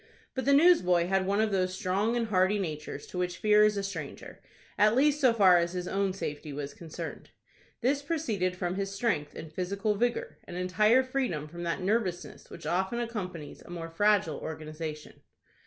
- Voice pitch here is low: No, high, 190 Hz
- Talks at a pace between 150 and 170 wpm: No, average, 180 wpm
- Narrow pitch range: No, average, 4.0 semitones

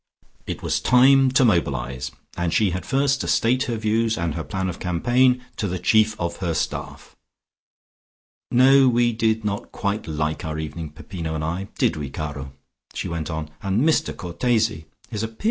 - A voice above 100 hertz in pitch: No, very low, 95 Hz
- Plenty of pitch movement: Yes, wide, 6.4 semitones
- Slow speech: No, average, 180 wpm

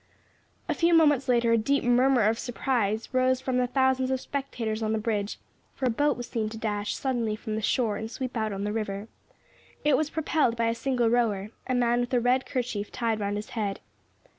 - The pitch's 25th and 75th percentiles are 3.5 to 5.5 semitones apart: No, average, 3.1 semitones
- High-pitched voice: Yes, high, 235 Hz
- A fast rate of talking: Yes, fast, 215 wpm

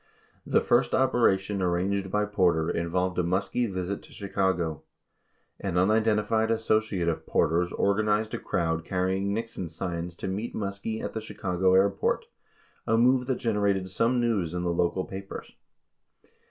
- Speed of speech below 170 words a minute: Yes, average, 155 wpm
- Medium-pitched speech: No, very low, 95 Hz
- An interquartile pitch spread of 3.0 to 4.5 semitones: Yes, average, 3.3 semitones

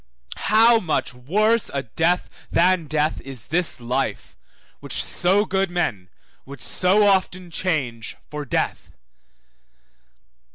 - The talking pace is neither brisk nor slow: No, slow, 115 wpm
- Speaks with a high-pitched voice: No, medium, 170 Hz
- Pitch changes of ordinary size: No, wide, 5.9 semitones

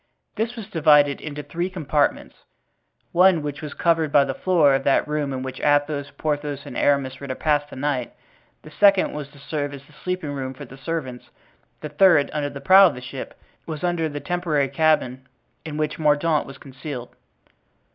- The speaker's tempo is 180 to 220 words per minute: Yes, average, 185 wpm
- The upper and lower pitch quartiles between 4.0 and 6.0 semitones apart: No, narrow, 2.5 semitones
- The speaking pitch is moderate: Yes, medium, 145 Hz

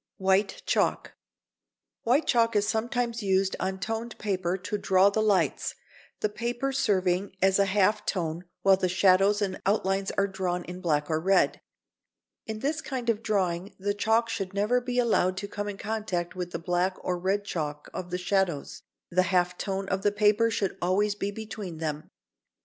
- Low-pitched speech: No, high, 195 Hz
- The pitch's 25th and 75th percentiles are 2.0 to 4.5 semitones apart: Yes, average, 2.7 semitones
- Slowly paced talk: No, average, 180 wpm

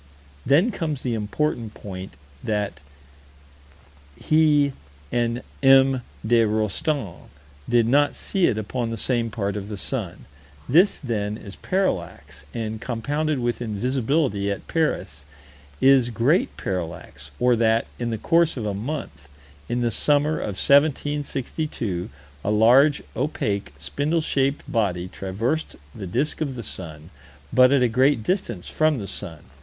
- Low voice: Yes, low, 120 Hz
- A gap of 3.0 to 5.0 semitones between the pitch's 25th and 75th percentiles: No, wide, 5.6 semitones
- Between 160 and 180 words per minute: No, average, 140 wpm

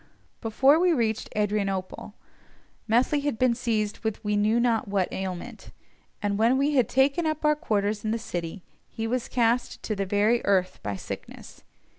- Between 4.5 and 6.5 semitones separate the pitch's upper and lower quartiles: No, average, 3.7 semitones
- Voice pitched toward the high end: Yes, high, 220 Hz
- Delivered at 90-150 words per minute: No, average, 170 wpm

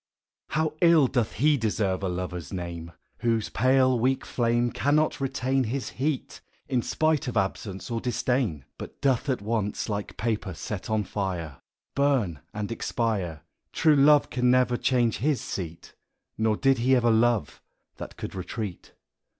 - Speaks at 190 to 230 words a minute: No, average, 150 wpm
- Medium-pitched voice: No, low, 115 Hz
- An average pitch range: Yes, average, 4.9 semitones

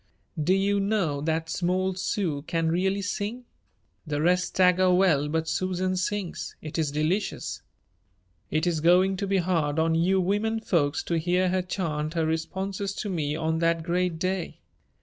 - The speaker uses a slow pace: No, average, 165 wpm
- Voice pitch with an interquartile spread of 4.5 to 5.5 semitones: No, average, 2.9 semitones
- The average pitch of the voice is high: No, medium, 180 Hz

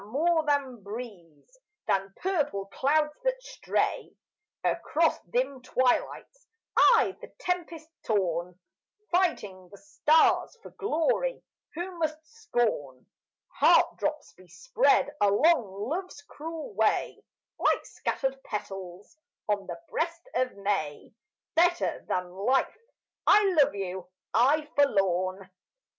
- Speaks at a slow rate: Yes, slow, 105 wpm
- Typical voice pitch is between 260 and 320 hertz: Yes, very high, 265 Hz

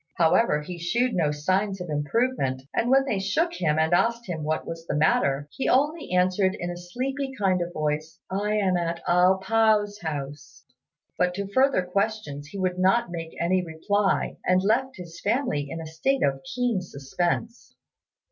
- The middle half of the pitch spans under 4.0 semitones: No, average, 5.2 semitones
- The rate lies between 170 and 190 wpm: Yes, average, 175 wpm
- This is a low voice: No, medium, 185 Hz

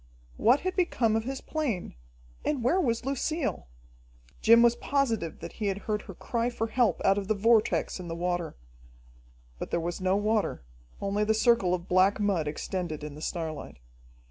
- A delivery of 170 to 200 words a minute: Yes, average, 180 wpm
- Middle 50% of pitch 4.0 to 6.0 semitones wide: Yes, average, 4.8 semitones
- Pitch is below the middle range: No, high, 210 Hz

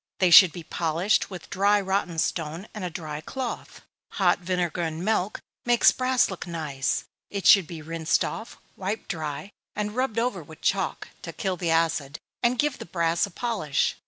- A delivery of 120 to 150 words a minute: No, average, 180 wpm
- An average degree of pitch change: Yes, average, 4.2 semitones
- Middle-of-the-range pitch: Yes, medium, 180 Hz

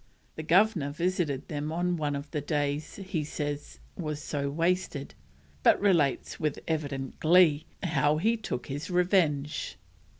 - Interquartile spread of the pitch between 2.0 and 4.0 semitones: Yes, average, 3.4 semitones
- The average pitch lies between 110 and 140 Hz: No, medium, 155 Hz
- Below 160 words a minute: Yes, average, 140 wpm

